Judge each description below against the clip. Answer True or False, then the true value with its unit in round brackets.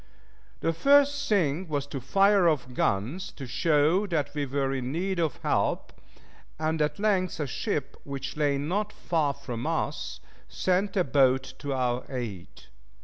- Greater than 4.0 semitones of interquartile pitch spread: True (5.2 semitones)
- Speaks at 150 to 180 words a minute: True (155 wpm)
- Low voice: False (150 Hz)